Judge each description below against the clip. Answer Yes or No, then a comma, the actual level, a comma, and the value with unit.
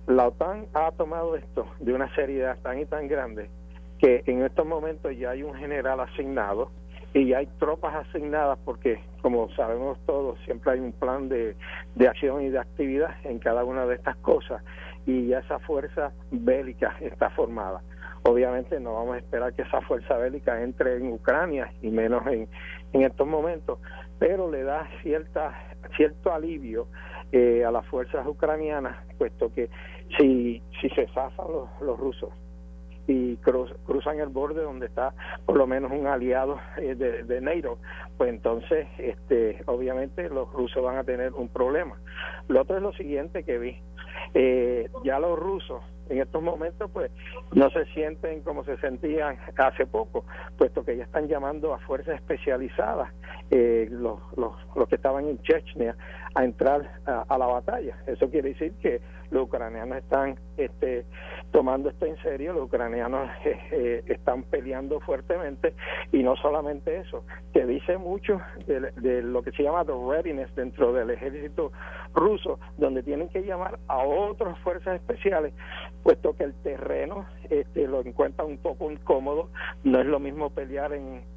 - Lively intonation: Yes, wide, 6.4 semitones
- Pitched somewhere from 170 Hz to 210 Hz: No, low, 135 Hz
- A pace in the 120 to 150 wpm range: No, average, 165 wpm